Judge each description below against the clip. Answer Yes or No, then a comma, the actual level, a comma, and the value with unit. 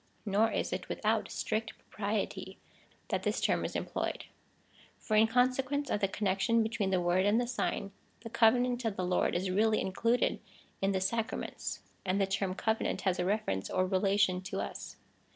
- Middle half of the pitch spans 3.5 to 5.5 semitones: No, average, 3.1 semitones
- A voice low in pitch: No, high, 205 Hz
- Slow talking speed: No, average, 175 wpm